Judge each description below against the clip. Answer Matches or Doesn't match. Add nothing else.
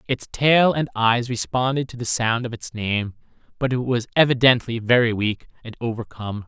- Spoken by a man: Matches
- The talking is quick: Doesn't match